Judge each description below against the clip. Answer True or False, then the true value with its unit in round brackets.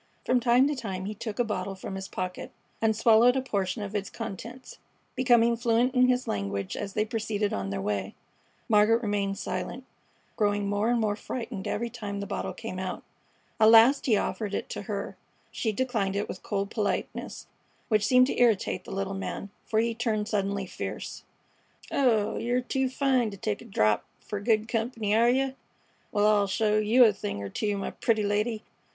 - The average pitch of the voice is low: False (215 Hz)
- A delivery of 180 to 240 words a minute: True (190 wpm)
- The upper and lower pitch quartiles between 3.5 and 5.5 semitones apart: False (2.9 semitones)